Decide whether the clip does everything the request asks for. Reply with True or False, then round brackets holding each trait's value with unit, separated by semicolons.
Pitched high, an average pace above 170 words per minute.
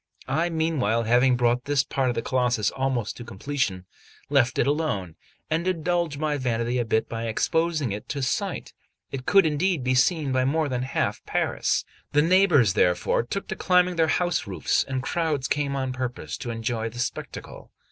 False (130 Hz; 180 wpm)